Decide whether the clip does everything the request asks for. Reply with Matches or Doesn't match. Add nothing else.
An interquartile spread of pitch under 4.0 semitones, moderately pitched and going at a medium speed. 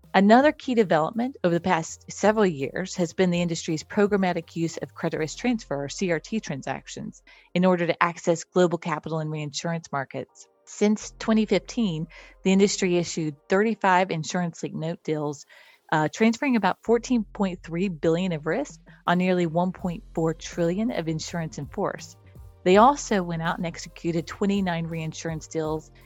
Matches